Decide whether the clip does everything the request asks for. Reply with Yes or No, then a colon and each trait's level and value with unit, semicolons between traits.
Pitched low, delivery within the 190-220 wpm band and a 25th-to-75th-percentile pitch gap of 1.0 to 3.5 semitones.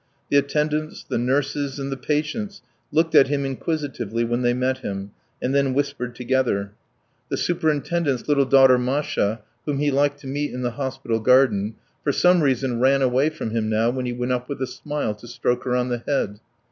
Yes: low, 130 Hz; average, 195 wpm; average, 2.9 semitones